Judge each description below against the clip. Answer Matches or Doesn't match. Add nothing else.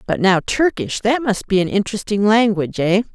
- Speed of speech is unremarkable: Matches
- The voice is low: Doesn't match